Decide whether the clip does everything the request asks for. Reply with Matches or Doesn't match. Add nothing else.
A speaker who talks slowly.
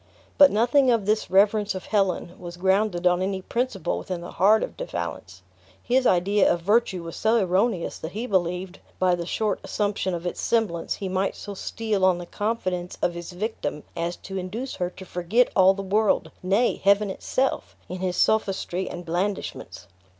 Doesn't match